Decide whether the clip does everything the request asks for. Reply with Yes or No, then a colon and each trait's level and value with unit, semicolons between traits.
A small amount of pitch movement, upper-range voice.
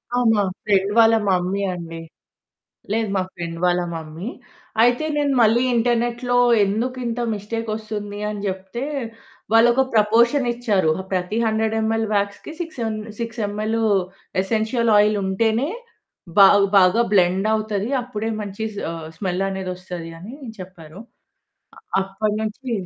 No: average, 3.3 semitones; high, 215 Hz